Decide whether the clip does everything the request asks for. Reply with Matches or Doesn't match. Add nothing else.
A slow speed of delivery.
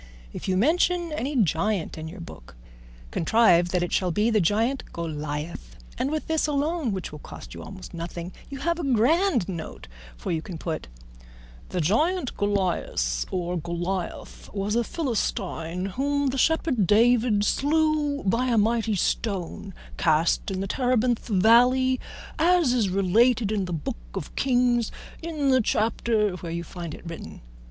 Doesn't match